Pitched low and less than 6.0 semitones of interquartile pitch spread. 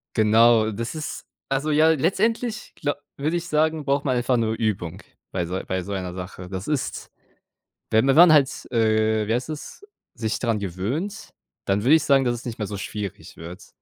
No: low, 115 Hz; wide, 6.6 semitones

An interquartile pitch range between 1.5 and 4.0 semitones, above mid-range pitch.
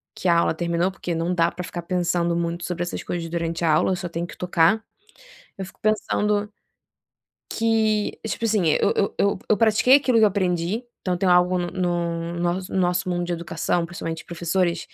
No: narrow, 2.5 semitones; medium, 175 Hz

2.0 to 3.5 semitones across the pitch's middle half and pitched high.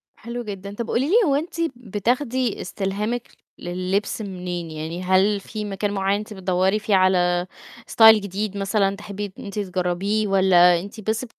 Yes: narrow, 2.6 semitones; high, 200 Hz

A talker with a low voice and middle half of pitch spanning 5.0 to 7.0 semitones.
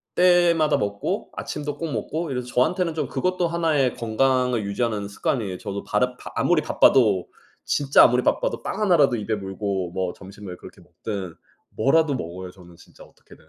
No: low, 125 Hz; wide, 7.4 semitones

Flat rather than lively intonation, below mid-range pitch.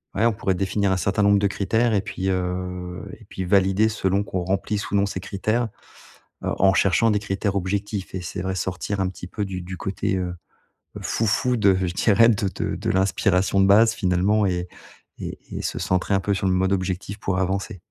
Yes: narrow, 1.7 semitones; very low, 95 Hz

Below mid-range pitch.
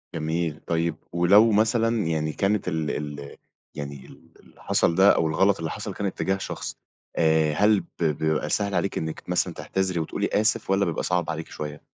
Yes: very low, 85 Hz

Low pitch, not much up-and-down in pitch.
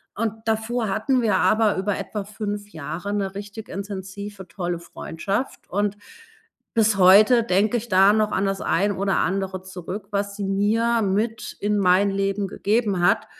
No: high, 200 Hz; narrow, 1.9 semitones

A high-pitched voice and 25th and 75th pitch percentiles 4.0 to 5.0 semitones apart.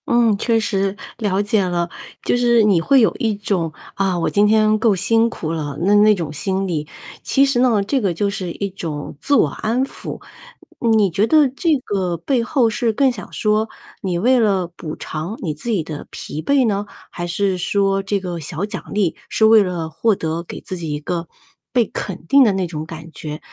Yes: high, 200 Hz; average, 4.6 semitones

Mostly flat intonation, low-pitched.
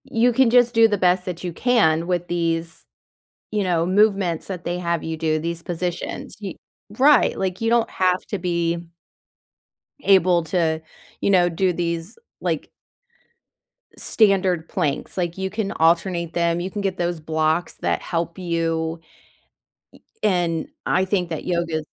No: narrow, 2.3 semitones; medium, 175 Hz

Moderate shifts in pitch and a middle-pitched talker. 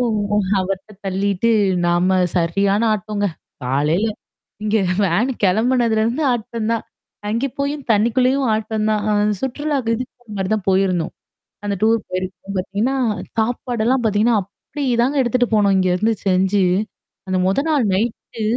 No: average, 3.9 semitones; high, 215 Hz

